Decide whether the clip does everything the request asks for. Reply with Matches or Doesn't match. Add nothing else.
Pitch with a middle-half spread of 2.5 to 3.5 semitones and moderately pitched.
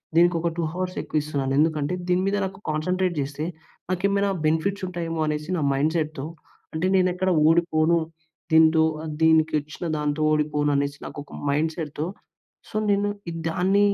Matches